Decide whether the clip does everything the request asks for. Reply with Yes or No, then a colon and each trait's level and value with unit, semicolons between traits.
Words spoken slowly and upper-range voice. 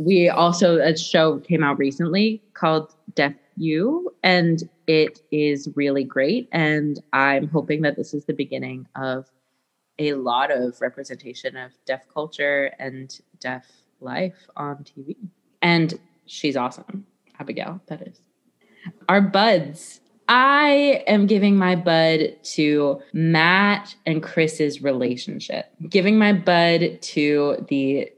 No: slow, 125 wpm; medium, 160 Hz